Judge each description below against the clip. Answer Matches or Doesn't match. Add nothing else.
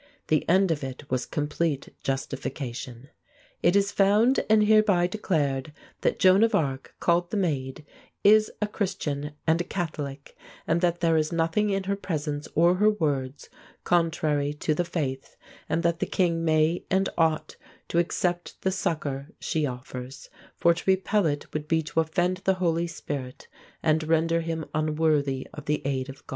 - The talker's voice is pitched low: Doesn't match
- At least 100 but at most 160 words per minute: Doesn't match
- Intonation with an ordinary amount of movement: Matches